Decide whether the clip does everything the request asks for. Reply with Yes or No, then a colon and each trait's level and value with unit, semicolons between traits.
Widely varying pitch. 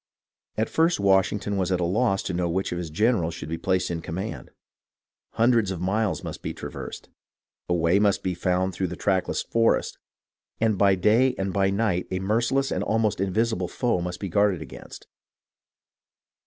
No: average, 3.4 semitones